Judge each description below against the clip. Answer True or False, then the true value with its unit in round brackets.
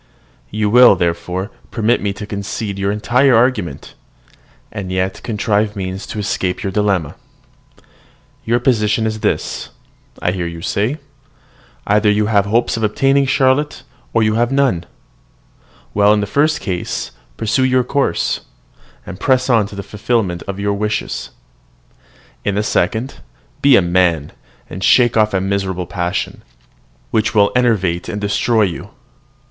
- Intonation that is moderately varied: True (3.6 semitones)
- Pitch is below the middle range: True (105 Hz)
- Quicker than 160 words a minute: False (145 wpm)